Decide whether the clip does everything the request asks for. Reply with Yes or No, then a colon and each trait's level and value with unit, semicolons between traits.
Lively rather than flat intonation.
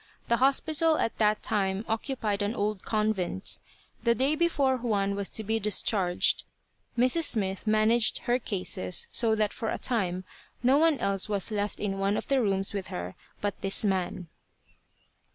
No: average, 3.5 semitones